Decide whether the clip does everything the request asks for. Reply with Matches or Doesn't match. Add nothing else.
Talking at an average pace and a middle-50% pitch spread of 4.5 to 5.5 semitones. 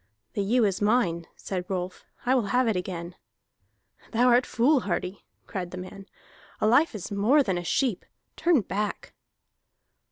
Matches